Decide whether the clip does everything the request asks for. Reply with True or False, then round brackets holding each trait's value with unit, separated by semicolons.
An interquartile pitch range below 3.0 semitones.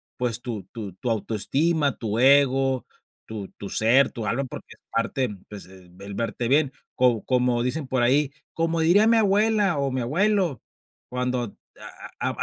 False (4.4 semitones)